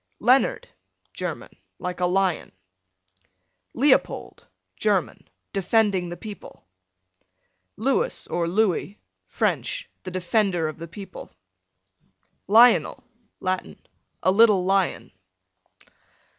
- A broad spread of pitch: No, average, 3.7 semitones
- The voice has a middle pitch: No, high, 195 Hz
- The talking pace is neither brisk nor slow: No, slow, 90 wpm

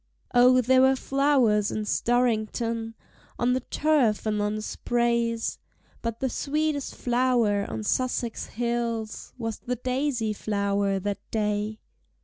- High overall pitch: Yes, high, 235 Hz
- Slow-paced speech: Yes, slow, 125 wpm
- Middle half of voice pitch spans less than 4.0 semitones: Yes, average, 2.9 semitones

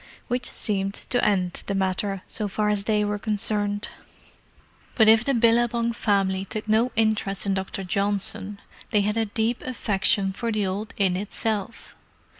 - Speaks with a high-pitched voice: Yes, high, 210 Hz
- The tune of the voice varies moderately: No, narrow, 2.2 semitones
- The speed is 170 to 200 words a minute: No, average, 160 wpm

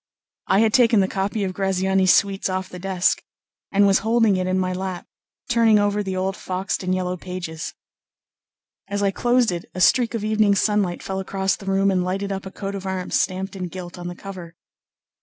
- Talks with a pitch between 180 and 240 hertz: Yes, high, 190 Hz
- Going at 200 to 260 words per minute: Yes, fast, 205 wpm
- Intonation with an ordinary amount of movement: No, narrow, 1.6 semitones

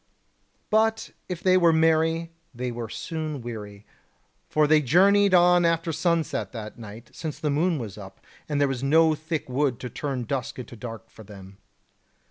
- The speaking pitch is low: No, medium, 150 Hz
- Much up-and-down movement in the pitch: Yes, wide, 5.9 semitones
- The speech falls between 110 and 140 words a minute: No, average, 170 wpm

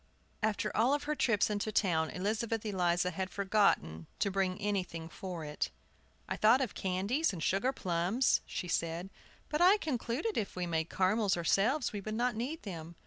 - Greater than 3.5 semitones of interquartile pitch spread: Yes, average, 4.6 semitones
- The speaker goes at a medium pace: Yes, average, 170 wpm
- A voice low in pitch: No, high, 200 Hz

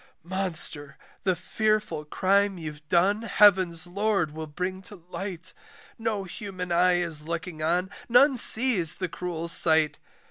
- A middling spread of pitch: Yes, average, 3.4 semitones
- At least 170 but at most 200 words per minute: No, slow, 135 wpm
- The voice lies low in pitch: No, medium, 180 Hz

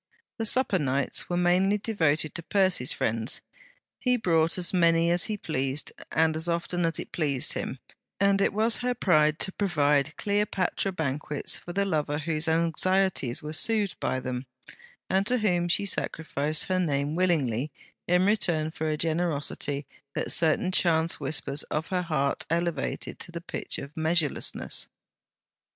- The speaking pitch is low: No, medium, 165 Hz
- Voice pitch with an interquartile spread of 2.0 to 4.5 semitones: Yes, average, 3.7 semitones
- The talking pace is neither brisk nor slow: Yes, average, 155 wpm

